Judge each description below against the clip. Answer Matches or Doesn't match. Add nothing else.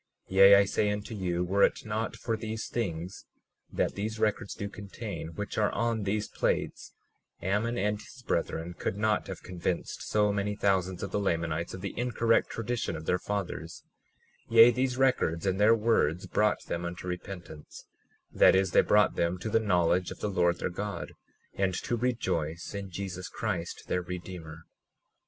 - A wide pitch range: Doesn't match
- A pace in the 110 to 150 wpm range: Doesn't match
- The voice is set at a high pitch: Doesn't match